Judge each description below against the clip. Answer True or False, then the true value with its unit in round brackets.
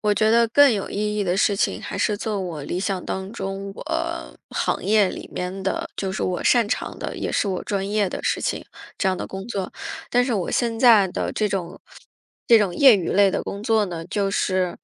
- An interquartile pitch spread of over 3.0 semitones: False (2.6 semitones)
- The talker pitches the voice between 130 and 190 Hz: False (200 Hz)